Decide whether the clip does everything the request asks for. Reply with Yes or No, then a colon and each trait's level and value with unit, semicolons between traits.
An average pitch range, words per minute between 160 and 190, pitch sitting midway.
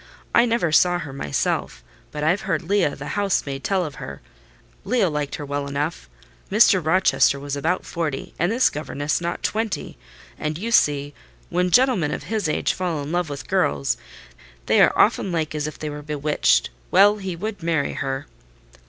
Yes: average, 4.6 semitones; average, 180 wpm; medium, 155 Hz